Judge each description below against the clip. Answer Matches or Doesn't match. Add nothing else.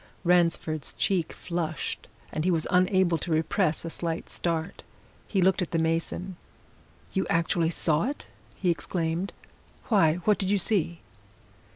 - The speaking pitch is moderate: Matches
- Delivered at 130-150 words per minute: Matches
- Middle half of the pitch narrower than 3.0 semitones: Matches